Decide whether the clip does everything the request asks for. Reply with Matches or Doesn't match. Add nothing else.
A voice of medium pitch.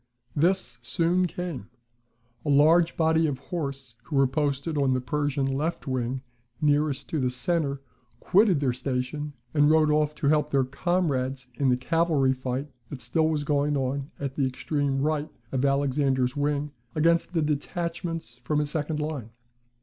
Matches